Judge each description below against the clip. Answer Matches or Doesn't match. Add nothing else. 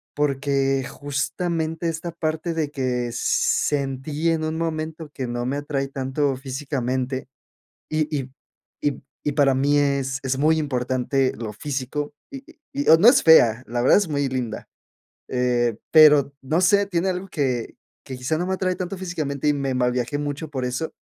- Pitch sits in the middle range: Matches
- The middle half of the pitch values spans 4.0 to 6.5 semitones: Doesn't match